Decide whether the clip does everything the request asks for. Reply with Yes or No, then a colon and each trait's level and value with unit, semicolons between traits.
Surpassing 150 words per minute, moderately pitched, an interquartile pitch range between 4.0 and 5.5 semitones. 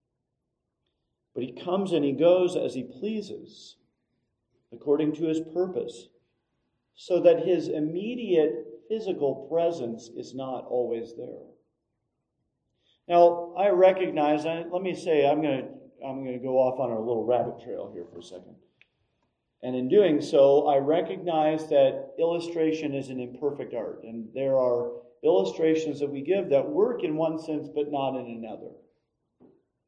No: average, 145 wpm; medium, 150 Hz; average, 5.0 semitones